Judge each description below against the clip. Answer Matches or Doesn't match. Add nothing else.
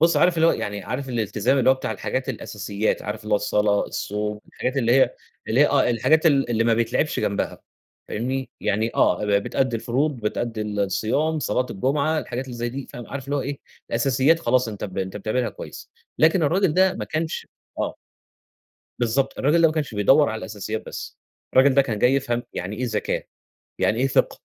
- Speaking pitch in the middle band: Doesn't match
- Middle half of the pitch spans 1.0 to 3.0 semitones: Doesn't match